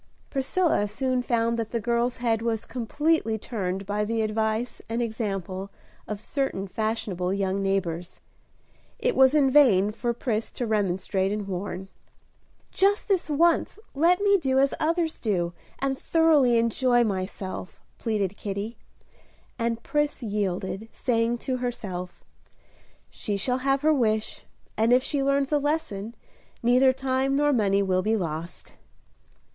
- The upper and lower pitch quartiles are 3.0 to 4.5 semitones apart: No, average, 5.0 semitones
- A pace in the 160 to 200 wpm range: No, average, 140 wpm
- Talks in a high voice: Yes, high, 230 Hz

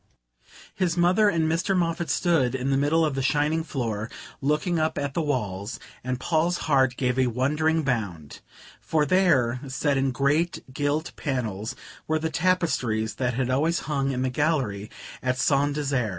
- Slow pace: No, average, 165 wpm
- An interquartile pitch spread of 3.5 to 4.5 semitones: Yes, average, 4.0 semitones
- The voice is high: No, medium, 140 Hz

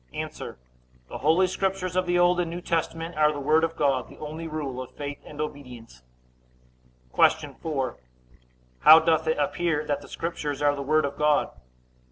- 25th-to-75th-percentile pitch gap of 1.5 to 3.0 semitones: Yes, narrow, 2.5 semitones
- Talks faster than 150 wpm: Yes, average, 180 wpm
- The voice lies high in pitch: No, medium, 155 Hz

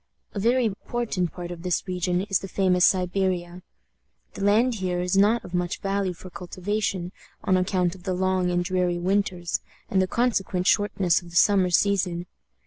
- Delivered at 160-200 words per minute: Yes, average, 175 wpm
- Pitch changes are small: Yes, narrow, 2.0 semitones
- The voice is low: No, medium, 185 Hz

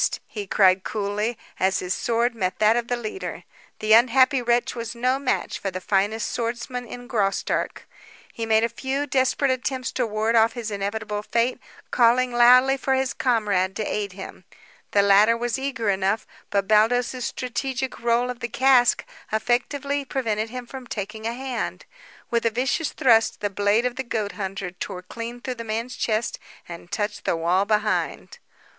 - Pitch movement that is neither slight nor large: Yes, average, 3.2 semitones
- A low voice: No, high, 230 Hz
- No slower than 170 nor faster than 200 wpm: Yes, average, 175 wpm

